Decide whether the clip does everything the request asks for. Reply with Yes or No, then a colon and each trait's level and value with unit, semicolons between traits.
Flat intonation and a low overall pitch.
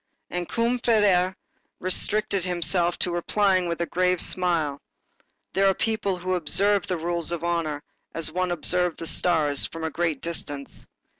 No: narrow, 1.9 semitones; medium, 175 Hz